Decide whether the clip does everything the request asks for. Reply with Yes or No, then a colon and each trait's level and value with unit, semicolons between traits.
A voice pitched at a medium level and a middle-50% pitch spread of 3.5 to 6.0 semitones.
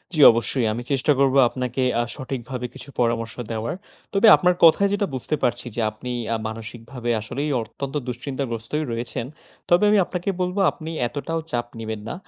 No: low, 125 Hz; average, 4.6 semitones